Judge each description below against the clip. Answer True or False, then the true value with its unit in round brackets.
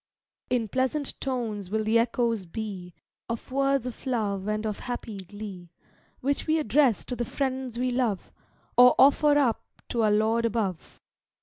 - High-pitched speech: True (230 Hz)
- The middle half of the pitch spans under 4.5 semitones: True (3.5 semitones)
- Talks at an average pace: True (160 wpm)